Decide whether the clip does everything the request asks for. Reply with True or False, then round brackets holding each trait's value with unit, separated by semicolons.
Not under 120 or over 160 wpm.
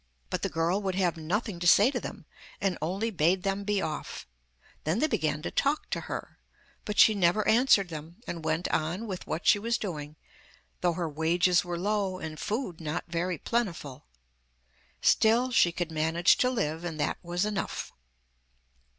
False (175 wpm)